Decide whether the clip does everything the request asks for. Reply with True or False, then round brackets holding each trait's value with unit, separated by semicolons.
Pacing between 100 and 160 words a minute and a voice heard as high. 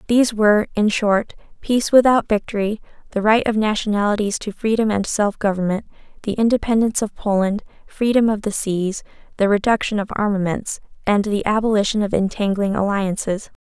True (150 wpm; 210 Hz)